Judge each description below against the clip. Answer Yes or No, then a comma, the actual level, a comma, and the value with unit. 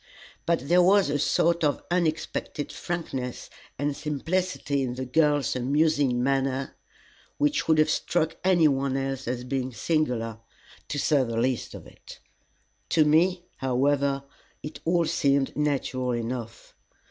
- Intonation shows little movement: No, average, 3.7 semitones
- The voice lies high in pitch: No, medium, 140 Hz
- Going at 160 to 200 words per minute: No, slow, 135 wpm